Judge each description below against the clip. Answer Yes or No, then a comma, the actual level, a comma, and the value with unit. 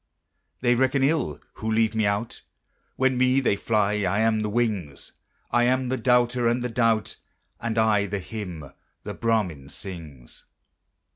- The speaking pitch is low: Yes, low, 110 Hz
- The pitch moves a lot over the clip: No, average, 3.3 semitones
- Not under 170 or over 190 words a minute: No, average, 155 wpm